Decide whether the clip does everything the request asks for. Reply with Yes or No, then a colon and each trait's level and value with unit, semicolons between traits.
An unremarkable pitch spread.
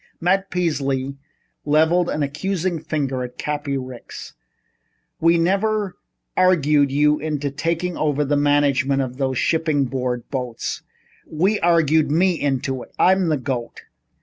Yes: average, 3.7 semitones